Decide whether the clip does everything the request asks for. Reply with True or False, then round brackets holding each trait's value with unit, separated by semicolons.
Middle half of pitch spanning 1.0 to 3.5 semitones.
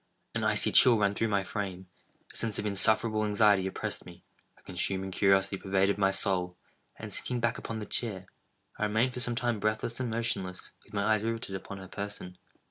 True (2.8 semitones)